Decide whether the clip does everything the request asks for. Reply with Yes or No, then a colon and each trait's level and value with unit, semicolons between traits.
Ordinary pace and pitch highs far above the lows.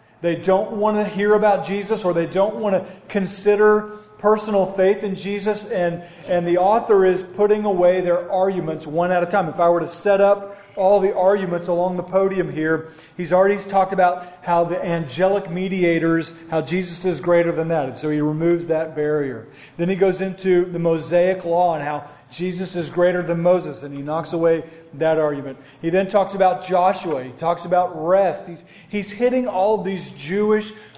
No: average, 190 wpm; average, 2.7 semitones